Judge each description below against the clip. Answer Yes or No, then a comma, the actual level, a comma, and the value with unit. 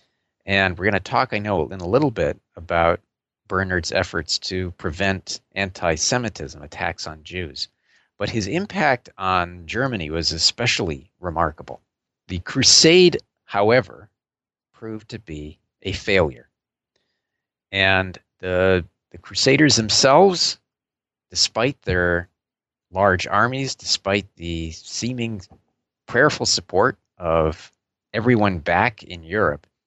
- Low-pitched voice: Yes, very low, 95 Hz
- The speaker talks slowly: Yes, slow, 115 wpm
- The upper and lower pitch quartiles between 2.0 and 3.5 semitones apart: No, average, 4.3 semitones